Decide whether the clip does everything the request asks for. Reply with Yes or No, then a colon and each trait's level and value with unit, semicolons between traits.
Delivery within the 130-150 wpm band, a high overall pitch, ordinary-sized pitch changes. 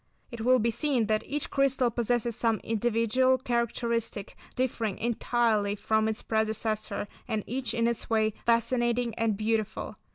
No: average, 140 wpm; high, 230 Hz; narrow, 1.7 semitones